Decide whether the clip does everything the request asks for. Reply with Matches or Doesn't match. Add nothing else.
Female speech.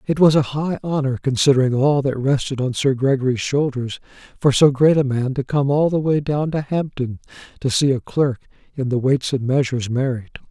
Doesn't match